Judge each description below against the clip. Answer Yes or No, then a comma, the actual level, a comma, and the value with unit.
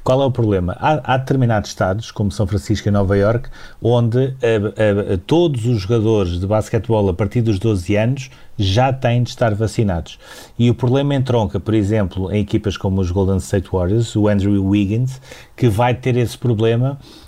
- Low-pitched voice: Yes, low, 110 Hz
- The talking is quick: Yes, fast, 190 wpm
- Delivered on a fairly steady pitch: No, average, 3.3 semitones